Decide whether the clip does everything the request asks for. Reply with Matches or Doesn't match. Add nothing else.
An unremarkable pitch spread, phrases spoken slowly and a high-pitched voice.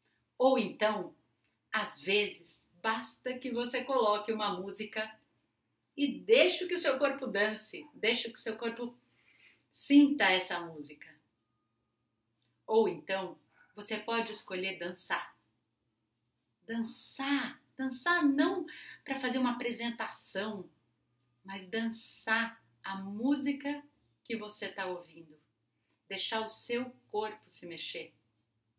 Doesn't match